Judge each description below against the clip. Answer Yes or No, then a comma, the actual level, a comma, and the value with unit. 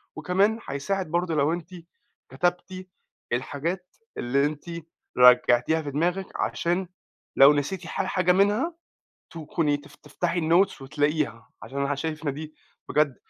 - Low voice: No, medium, 160 Hz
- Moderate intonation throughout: Yes, average, 4.0 semitones